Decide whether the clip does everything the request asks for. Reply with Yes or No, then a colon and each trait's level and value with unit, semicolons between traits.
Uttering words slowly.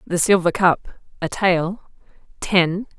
Yes: slow, 120 wpm